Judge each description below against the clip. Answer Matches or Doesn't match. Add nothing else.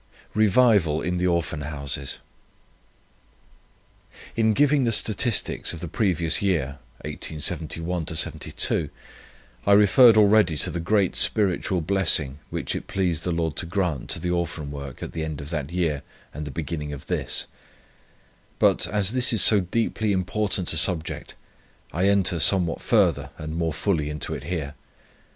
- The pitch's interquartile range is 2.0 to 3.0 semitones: Doesn't match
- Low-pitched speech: Matches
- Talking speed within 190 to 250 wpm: Doesn't match